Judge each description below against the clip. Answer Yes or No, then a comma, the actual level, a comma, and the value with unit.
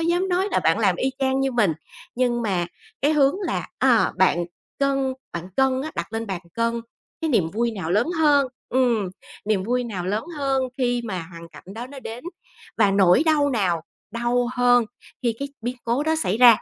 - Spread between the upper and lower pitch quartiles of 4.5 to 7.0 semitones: Yes, average, 4.8 semitones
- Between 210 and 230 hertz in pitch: No, high, 240 Hz